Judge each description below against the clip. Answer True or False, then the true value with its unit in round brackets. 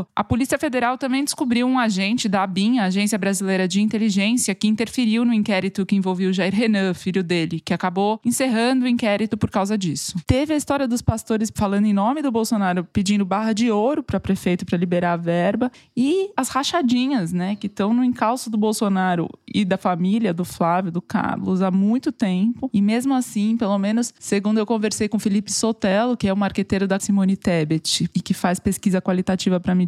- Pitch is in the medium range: False (205 Hz)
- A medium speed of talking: False (200 wpm)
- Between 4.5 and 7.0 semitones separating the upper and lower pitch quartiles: False (3.6 semitones)